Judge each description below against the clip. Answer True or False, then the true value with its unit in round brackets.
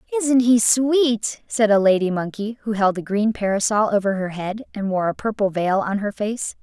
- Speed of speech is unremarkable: False (210 wpm)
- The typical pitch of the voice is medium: False (210 Hz)